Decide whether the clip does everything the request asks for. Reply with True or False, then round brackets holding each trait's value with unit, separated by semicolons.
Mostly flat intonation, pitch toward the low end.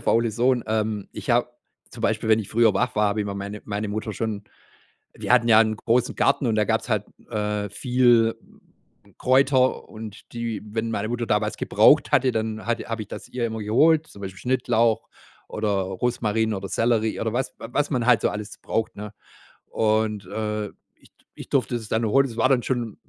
True (2.3 semitones; 110 Hz)